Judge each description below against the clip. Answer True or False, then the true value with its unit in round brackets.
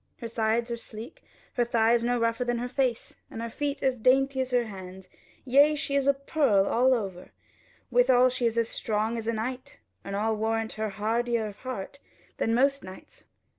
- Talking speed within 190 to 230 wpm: True (200 wpm)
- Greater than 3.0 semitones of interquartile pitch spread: False (2.6 semitones)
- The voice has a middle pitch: False (235 Hz)